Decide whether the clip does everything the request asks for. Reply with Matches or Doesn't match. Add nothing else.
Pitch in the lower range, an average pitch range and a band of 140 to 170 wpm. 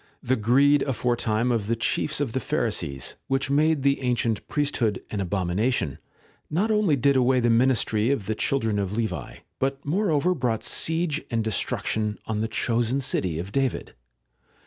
Matches